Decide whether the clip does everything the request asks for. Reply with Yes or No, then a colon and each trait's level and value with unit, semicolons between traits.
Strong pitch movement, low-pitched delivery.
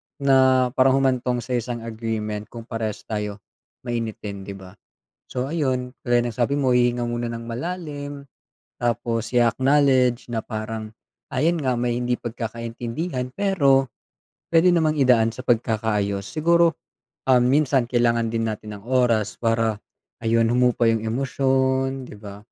No: average, 2.7 semitones; low, 120 Hz